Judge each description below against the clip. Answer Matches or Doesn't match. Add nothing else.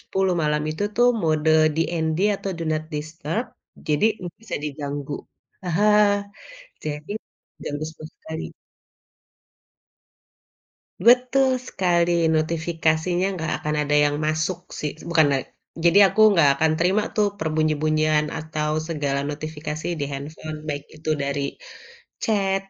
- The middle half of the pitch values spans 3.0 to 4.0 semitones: Doesn't match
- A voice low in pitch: Doesn't match